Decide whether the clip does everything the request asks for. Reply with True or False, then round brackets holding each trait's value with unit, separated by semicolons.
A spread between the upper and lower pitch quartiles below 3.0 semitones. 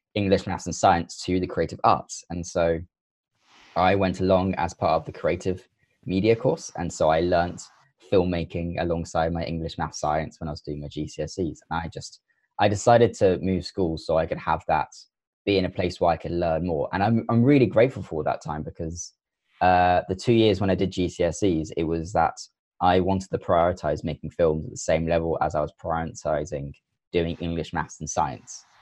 True (2.5 semitones)